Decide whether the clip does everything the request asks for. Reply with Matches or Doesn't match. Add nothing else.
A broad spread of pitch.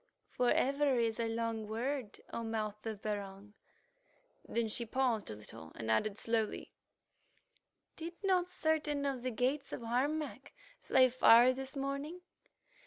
Doesn't match